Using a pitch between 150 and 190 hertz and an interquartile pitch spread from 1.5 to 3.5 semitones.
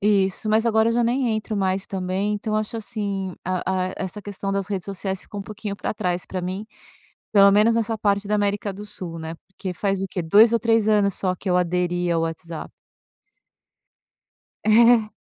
No: high, 200 Hz; narrow, 2.5 semitones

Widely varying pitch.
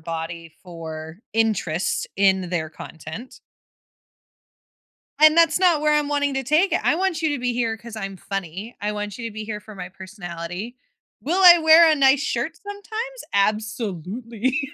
Yes: wide, 8.3 semitones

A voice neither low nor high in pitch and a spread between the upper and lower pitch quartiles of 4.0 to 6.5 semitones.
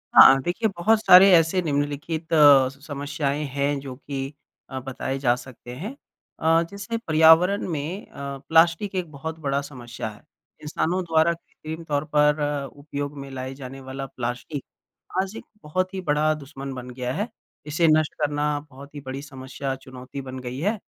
No: medium, 145 Hz; average, 3.3 semitones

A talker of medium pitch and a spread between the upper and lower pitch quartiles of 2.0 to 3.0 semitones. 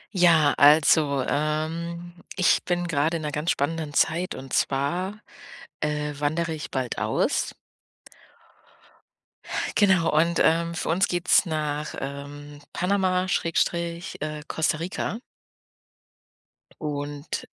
Yes: medium, 160 Hz; average, 2.7 semitones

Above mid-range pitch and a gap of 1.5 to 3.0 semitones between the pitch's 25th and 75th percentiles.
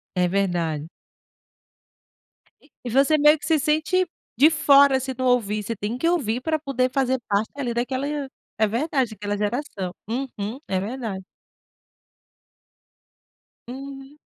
No: very high, 255 Hz; average, 5.2 semitones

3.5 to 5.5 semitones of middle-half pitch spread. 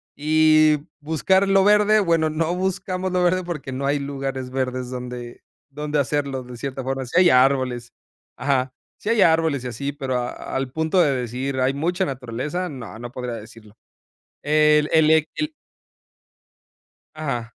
Yes: average, 4.1 semitones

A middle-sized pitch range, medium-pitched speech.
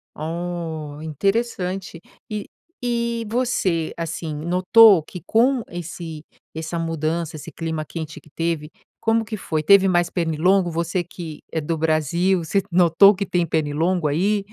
Yes: average, 3.4 semitones; medium, 170 Hz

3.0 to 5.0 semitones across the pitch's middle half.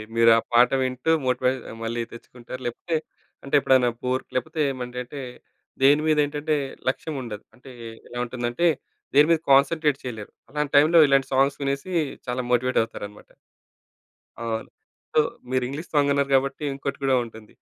No: narrow, 2.6 semitones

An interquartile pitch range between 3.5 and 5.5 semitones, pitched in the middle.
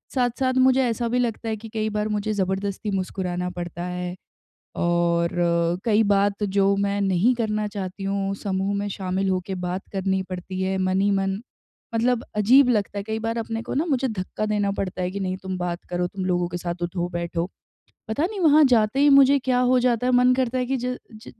No: average, 4.2 semitones; high, 200 Hz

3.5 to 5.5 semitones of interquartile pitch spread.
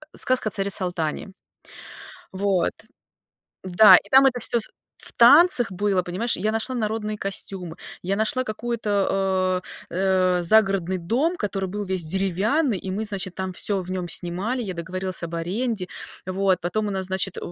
No: average, 2.9 semitones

